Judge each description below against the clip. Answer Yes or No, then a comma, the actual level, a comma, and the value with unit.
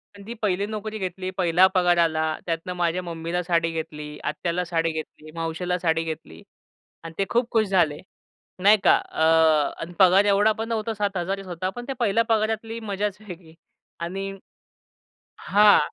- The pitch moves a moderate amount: Yes, average, 3.8 semitones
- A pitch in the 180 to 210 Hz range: Yes, medium, 185 Hz